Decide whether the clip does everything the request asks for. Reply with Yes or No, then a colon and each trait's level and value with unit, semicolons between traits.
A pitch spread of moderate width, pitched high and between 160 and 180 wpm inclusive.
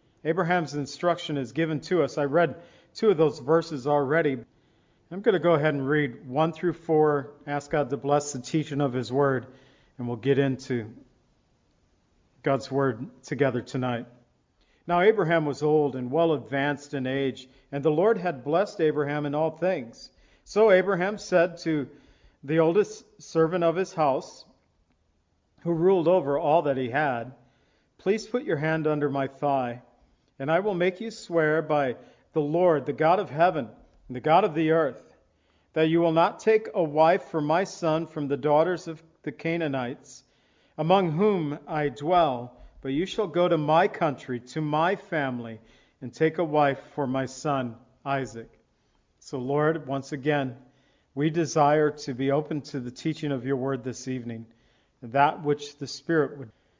No: average, 3.4 semitones; medium, 150 Hz; average, 170 wpm